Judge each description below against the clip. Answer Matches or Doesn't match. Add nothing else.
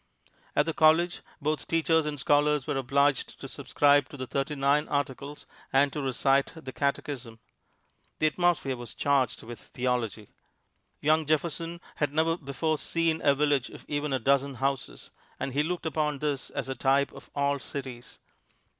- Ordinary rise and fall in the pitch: Doesn't match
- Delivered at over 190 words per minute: Doesn't match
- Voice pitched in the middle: Matches